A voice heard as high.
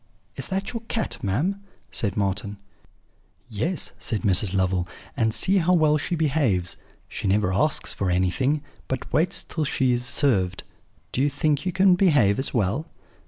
No: low, 130 Hz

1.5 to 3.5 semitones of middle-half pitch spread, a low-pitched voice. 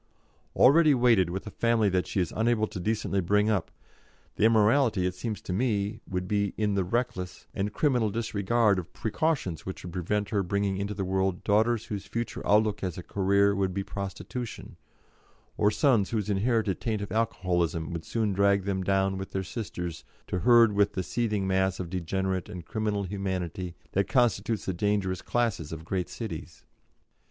Yes: average, 2.9 semitones; low, 100 Hz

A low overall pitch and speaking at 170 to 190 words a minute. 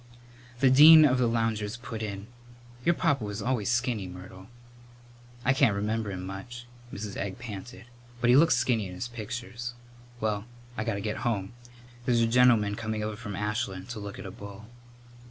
Yes: low, 110 Hz; average, 180 wpm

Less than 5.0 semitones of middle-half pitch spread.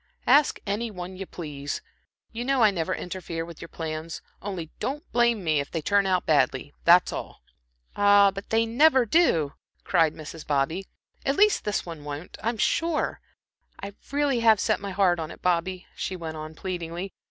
No: average, 5.3 semitones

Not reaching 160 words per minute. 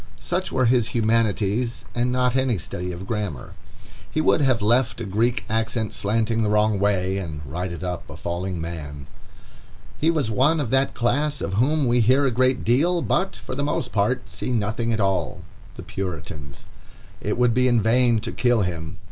No: average, 180 wpm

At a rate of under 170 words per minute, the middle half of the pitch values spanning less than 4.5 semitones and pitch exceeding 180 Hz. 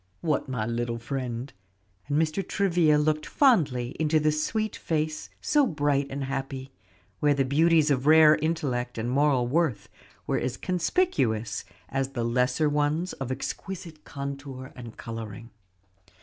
No: average, 140 wpm; average, 3.7 semitones; medium, 140 Hz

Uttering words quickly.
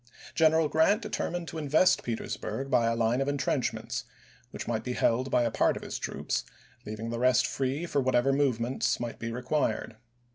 No: average, 185 wpm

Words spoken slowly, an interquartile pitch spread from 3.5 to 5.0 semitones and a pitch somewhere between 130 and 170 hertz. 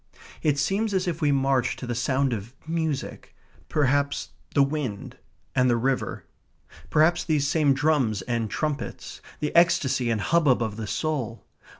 No: average, 155 wpm; average, 4.2 semitones; medium, 140 Hz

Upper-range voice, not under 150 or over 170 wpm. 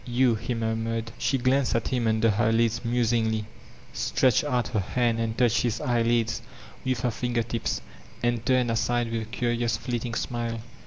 No: low, 115 Hz; average, 165 wpm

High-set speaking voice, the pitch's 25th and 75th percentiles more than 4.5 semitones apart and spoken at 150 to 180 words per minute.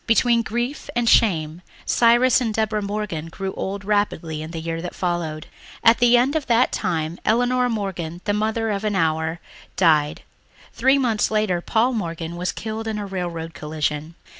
Yes: high, 200 Hz; wide, 5.6 semitones; average, 170 wpm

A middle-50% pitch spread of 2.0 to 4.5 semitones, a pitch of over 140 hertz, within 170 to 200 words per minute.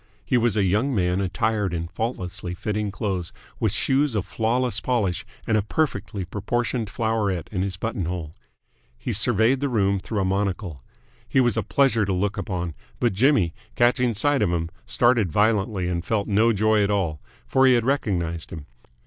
No: average, 4.2 semitones; low, 105 Hz; average, 175 wpm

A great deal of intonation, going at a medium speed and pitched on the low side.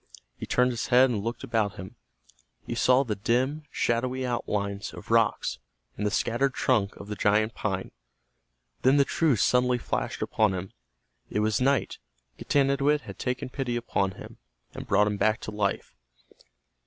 No: average, 3.8 semitones; average, 165 wpm; low, 120 Hz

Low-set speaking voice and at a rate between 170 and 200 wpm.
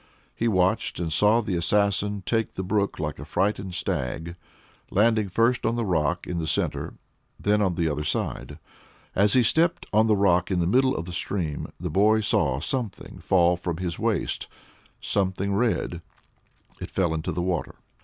Yes: very low, 95 Hz; average, 175 wpm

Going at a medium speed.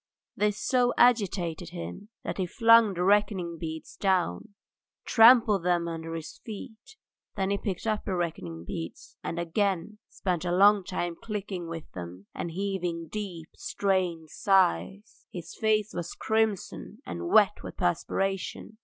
Yes: average, 145 wpm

